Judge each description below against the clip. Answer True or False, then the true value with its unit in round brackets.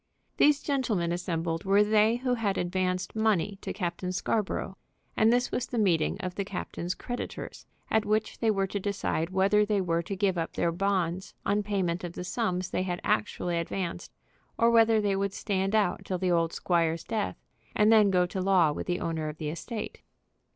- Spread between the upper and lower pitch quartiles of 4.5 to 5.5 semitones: False (3.2 semitones)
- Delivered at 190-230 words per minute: True (195 wpm)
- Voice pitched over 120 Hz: True (190 Hz)